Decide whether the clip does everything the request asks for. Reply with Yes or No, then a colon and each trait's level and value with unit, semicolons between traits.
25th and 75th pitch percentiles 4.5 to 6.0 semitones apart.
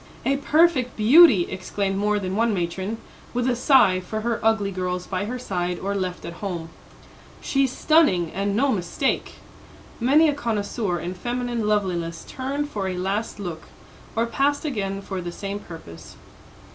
Yes: average, 5.0 semitones